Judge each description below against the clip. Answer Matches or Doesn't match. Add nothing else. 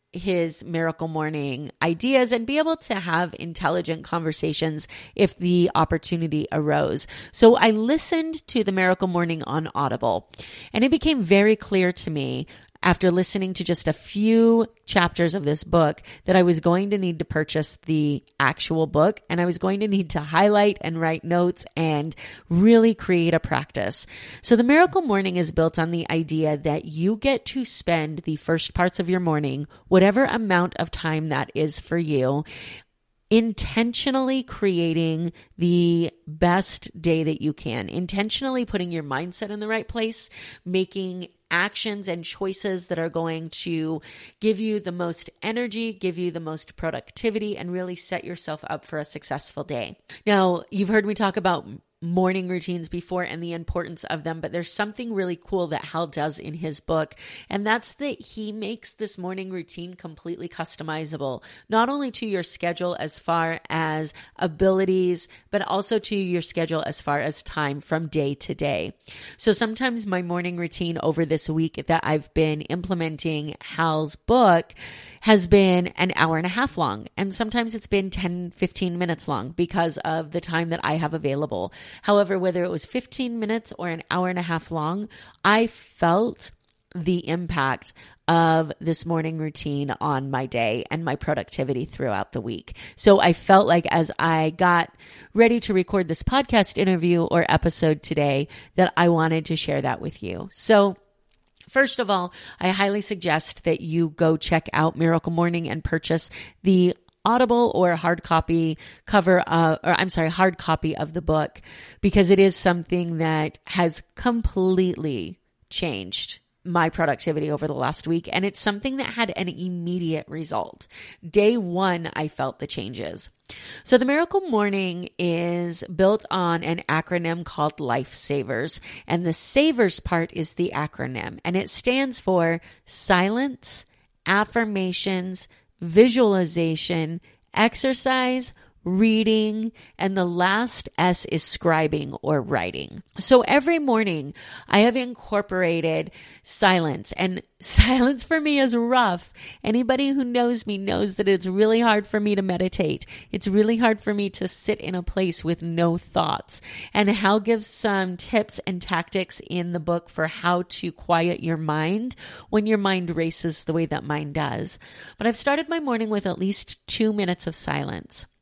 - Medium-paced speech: Matches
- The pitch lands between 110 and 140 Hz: Doesn't match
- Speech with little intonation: Doesn't match